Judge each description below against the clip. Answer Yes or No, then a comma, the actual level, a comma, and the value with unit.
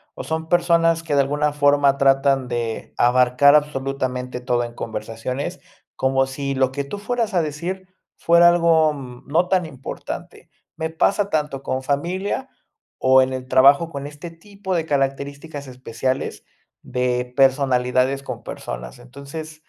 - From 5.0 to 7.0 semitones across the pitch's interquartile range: No, average, 3.7 semitones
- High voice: No, medium, 140 Hz